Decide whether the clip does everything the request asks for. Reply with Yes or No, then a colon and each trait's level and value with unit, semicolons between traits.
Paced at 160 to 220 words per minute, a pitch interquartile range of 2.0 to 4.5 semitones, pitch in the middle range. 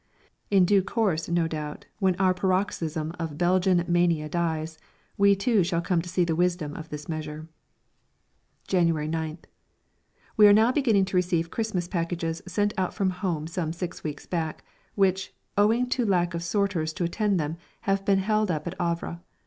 Yes: average, 175 wpm; average, 3.1 semitones; medium, 175 Hz